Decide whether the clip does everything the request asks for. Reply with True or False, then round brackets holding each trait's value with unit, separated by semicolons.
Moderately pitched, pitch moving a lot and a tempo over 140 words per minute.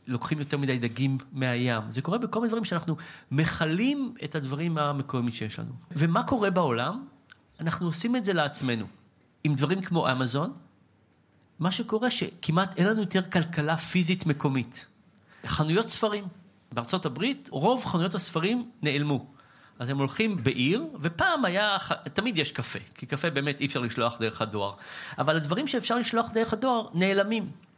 True (160 Hz; 6.7 semitones; 150 wpm)